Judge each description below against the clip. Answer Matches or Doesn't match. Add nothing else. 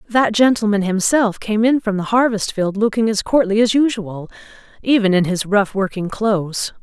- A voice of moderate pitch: Doesn't match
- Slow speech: Doesn't match